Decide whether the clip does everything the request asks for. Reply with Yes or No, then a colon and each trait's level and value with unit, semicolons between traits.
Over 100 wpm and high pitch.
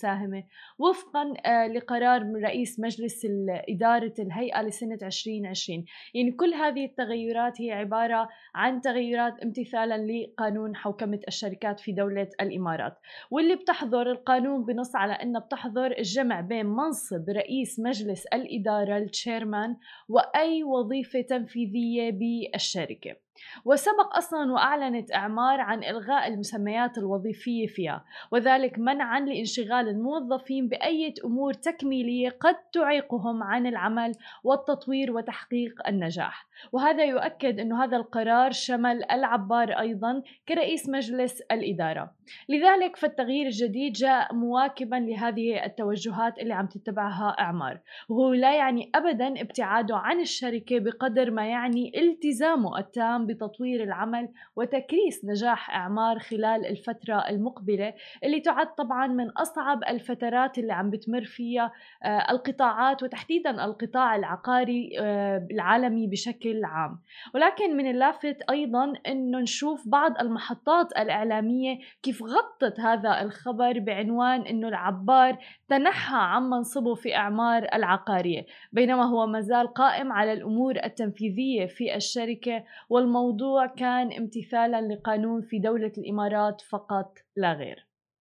Yes: average, 115 wpm; high, 235 Hz